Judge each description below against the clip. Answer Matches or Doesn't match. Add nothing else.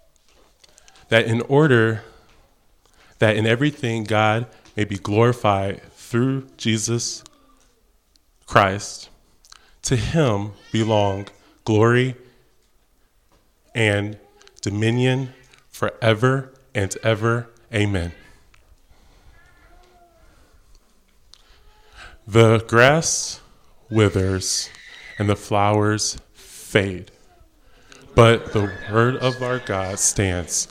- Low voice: Matches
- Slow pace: Matches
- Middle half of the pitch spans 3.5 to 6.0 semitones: Doesn't match